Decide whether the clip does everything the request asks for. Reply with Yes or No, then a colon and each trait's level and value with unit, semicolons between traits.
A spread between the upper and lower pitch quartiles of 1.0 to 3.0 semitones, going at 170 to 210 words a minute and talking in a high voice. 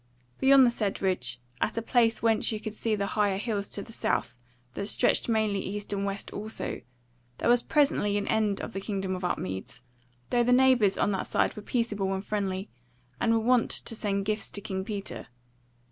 Yes: narrow, 2.6 semitones; average, 200 wpm; high, 210 Hz